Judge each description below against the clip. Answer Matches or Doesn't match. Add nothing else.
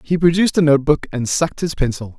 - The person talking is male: Matches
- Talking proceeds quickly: Matches